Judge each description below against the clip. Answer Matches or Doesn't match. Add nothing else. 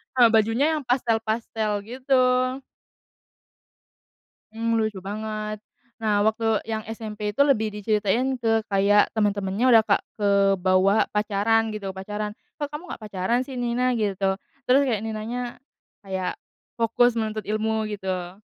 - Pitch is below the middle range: Doesn't match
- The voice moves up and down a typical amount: Doesn't match